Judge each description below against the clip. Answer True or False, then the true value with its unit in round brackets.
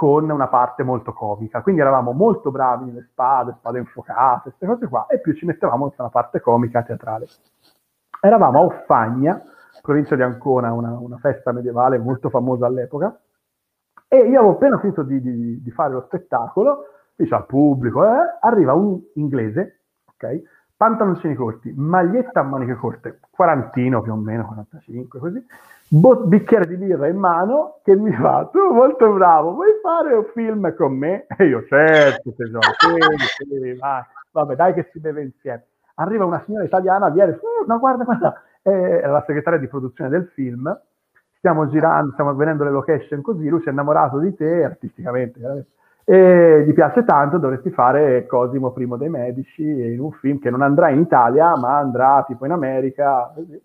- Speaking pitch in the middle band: True (145 Hz)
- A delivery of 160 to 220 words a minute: True (170 wpm)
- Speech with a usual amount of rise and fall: False (6.5 semitones)